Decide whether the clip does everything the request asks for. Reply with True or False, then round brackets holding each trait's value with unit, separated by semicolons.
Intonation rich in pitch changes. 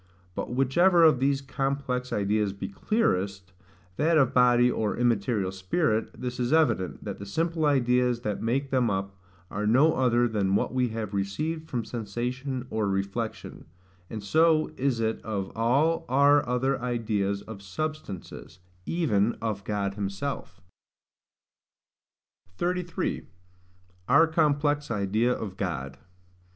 True (5.7 semitones)